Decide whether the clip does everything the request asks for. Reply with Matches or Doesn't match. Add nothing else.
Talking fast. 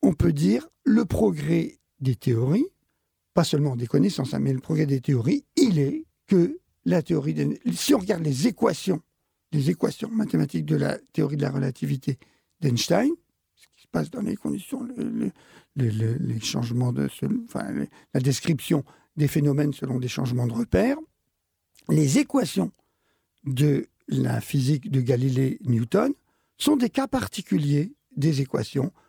Doesn't match